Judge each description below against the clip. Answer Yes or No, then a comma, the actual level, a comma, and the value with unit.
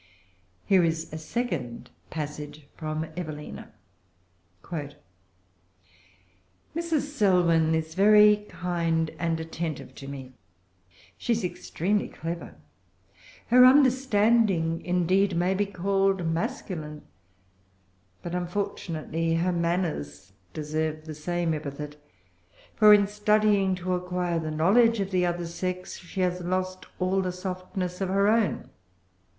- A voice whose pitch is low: No, medium, 175 Hz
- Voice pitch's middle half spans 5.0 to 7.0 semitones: No, average, 3.8 semitones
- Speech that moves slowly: Yes, slow, 110 wpm